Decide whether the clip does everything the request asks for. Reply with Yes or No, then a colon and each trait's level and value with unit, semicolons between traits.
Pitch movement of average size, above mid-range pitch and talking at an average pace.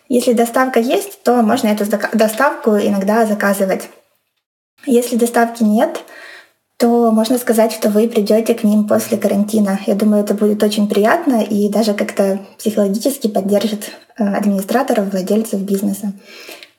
No: narrow, 2.3 semitones; high, 215 Hz; average, 130 wpm